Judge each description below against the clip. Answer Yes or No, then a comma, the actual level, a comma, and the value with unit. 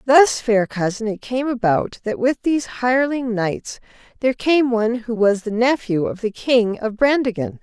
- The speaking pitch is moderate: No, high, 230 Hz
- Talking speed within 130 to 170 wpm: No, average, 180 wpm